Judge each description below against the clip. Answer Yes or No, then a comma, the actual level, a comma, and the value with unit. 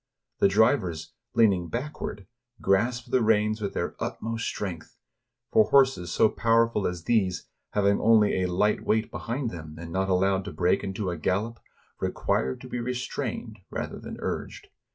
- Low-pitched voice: Yes, low, 105 Hz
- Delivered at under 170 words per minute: Yes, average, 155 wpm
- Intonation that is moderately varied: Yes, average, 3.8 semitones